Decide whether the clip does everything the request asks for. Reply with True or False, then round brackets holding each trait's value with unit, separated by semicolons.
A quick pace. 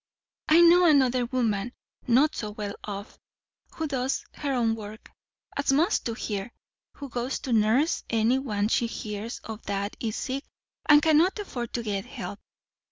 False (165 wpm)